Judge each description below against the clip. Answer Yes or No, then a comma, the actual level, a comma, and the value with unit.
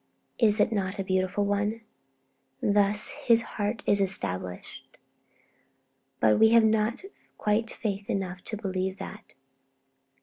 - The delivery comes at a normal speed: No, slow, 125 wpm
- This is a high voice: Yes, high, 205 Hz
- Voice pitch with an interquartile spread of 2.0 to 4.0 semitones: Yes, narrow, 2.4 semitones